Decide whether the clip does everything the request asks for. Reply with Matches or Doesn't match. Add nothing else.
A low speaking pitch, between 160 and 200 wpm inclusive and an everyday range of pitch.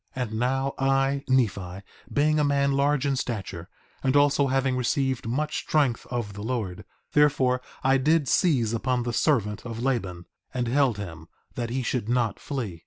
Matches